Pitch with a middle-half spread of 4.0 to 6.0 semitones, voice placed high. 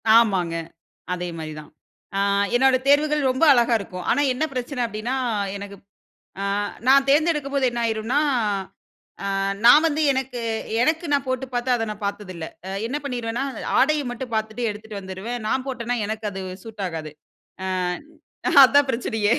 Yes: average, 4.3 semitones; high, 240 Hz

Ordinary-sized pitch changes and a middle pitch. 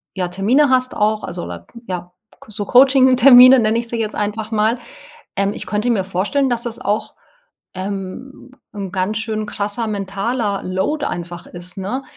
No: average, 4.1 semitones; high, 215 Hz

